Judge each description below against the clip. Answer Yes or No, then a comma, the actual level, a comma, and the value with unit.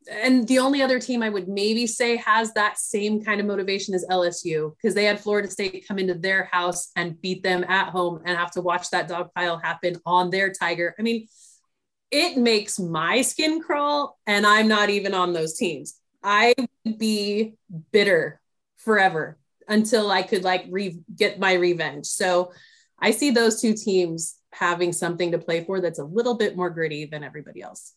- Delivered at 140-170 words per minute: No, average, 190 wpm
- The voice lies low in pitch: No, high, 195 Hz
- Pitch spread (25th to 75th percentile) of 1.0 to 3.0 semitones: No, average, 3.8 semitones